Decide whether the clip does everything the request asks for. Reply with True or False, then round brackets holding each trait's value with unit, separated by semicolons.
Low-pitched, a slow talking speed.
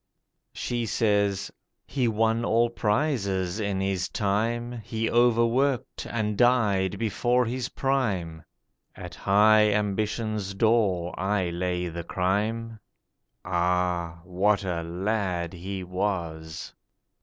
True (100 Hz; 105 wpm)